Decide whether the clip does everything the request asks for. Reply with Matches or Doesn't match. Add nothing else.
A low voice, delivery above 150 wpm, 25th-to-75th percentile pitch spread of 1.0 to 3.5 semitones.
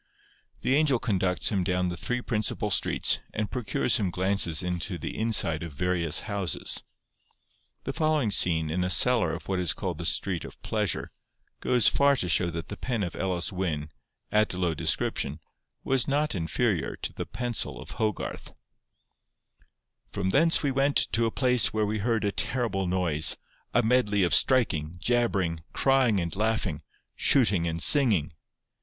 Doesn't match